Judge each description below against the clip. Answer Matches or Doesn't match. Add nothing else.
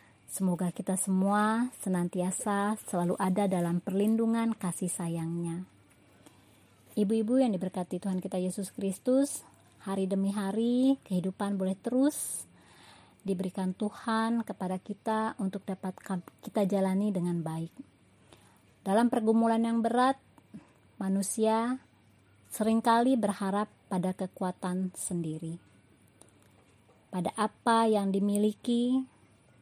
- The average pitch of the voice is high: Matches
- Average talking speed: Matches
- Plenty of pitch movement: Doesn't match